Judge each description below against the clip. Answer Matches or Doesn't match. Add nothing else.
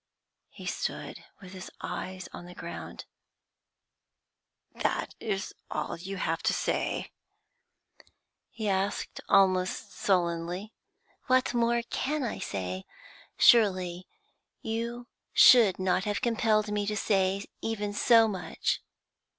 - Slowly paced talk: Matches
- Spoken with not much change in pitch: Doesn't match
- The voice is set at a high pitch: Matches